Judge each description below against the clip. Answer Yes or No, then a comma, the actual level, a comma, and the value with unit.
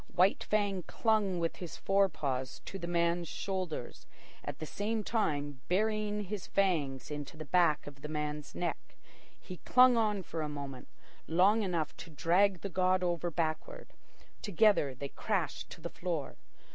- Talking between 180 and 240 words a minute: No, average, 160 wpm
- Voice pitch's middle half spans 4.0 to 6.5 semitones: Yes, average, 4.8 semitones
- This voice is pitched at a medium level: Yes, medium, 175 Hz